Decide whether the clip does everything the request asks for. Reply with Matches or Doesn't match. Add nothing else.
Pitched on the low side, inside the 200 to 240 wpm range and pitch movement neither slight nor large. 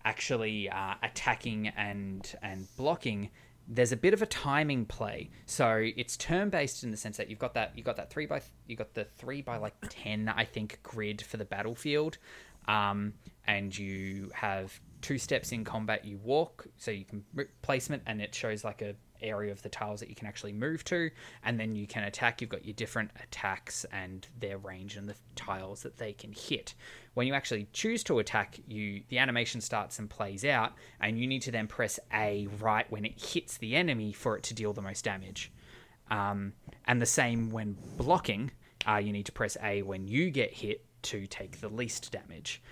Matches